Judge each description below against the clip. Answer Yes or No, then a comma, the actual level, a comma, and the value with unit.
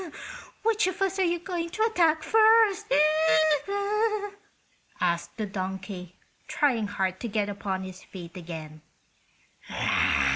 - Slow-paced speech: Yes, slow, 115 wpm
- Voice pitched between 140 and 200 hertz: No, high, 215 Hz